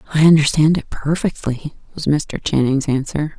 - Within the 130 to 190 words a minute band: Yes, average, 140 wpm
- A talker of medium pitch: Yes, medium, 150 Hz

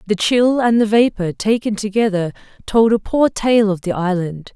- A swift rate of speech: No, average, 185 wpm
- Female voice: Yes, female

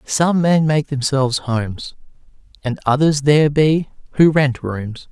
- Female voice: No, male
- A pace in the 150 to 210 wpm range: No, average, 140 wpm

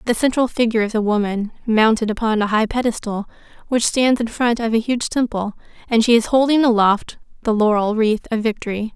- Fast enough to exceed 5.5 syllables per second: Yes, 5.7 syllables/s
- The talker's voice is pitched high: Yes, high, 225 Hz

